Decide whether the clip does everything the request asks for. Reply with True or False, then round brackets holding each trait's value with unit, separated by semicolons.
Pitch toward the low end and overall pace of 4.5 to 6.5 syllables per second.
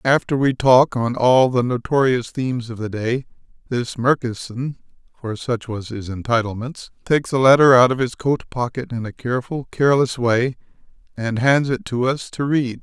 True (125 Hz; 4.9 syllables/s)